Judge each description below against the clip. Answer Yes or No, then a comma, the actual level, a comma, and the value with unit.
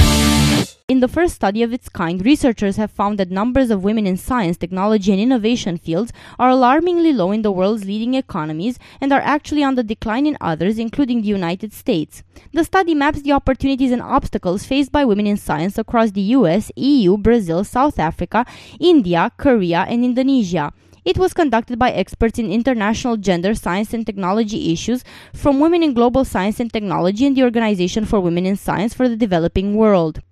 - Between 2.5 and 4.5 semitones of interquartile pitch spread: No, wide, 5.4 semitones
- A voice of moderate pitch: No, high, 225 Hz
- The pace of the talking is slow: No, average, 185 wpm